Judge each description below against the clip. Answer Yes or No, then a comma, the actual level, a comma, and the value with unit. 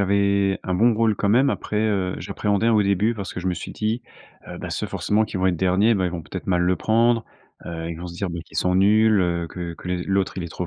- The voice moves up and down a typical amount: Yes, average, 3.1 semitones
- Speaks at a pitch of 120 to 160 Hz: No, very low, 95 Hz